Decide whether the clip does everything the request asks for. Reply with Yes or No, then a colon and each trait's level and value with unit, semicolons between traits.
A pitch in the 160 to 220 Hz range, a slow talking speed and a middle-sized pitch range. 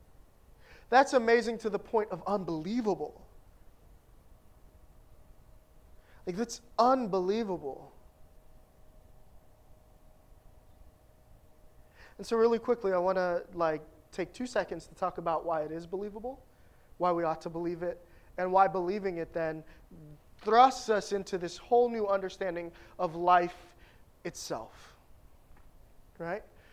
Yes: medium, 185 Hz; slow, 110 wpm; average, 4.2 semitones